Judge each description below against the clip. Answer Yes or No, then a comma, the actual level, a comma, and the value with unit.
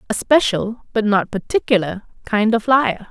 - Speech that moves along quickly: No, average, 155 wpm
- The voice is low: No, high, 220 Hz